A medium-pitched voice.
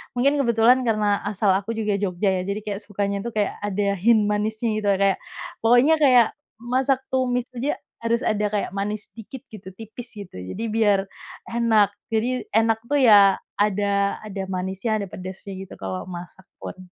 No: high, 210 Hz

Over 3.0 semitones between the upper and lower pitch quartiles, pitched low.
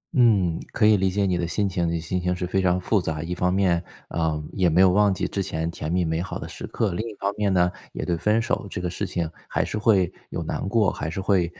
No: narrow, 2.6 semitones; very low, 90 Hz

